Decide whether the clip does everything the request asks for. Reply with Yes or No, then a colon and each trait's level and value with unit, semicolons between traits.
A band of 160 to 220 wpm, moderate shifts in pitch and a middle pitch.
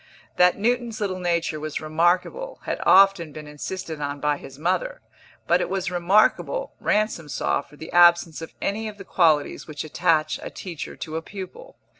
Yes: average, 175 wpm; average, 4.2 semitones; medium, 175 Hz